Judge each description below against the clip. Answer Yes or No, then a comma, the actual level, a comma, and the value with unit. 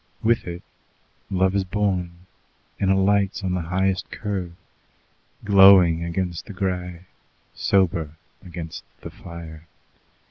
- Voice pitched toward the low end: Yes, very low, 90 Hz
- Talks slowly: Yes, slow, 110 wpm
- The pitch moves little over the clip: Yes, narrow, 2.2 semitones